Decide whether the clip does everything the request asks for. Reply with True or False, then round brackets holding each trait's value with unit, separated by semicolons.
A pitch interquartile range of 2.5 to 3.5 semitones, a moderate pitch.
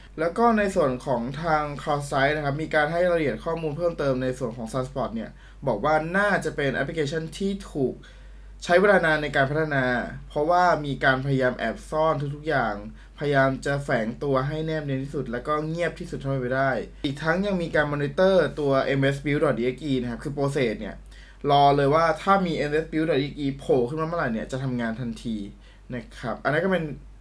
True (3.2 semitones; 145 Hz)